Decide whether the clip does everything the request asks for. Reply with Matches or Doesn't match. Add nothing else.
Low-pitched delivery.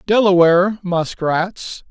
Doesn't match